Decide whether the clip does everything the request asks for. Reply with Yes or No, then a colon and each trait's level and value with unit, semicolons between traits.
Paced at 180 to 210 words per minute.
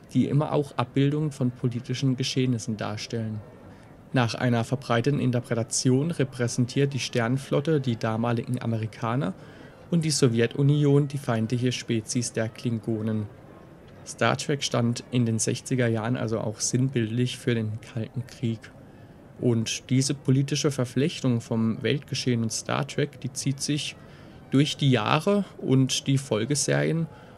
No: slow, 125 wpm